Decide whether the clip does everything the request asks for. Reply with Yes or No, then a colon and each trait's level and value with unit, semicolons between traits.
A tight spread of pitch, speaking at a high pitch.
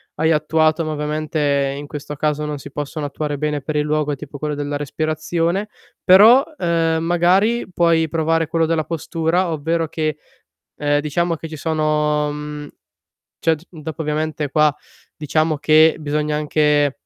No: narrow, 1.6 semitones; medium, 155 Hz